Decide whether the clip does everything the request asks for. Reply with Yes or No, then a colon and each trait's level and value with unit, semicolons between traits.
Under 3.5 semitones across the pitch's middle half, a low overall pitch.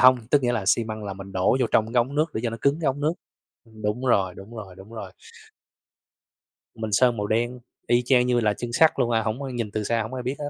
Yes: average, 3.0 semitones; low, 115 Hz